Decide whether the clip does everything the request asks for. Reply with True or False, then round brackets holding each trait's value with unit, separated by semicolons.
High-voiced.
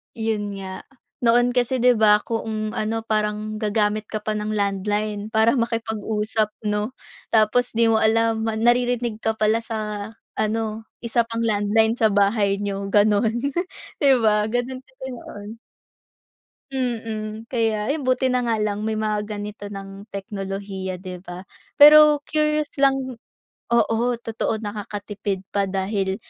True (215 Hz)